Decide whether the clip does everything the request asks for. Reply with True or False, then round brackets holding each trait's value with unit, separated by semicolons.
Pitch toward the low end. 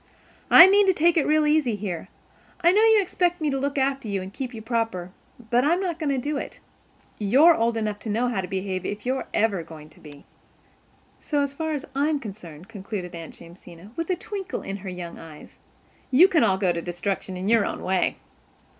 False (230 Hz)